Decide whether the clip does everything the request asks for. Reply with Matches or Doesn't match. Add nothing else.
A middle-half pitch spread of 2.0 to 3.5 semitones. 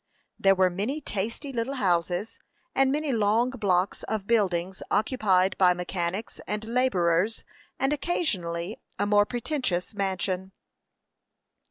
Doesn't match